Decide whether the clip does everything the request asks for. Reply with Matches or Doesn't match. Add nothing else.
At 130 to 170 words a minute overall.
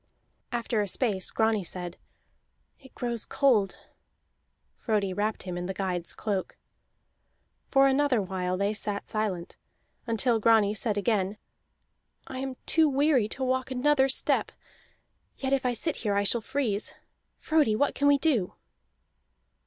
Matches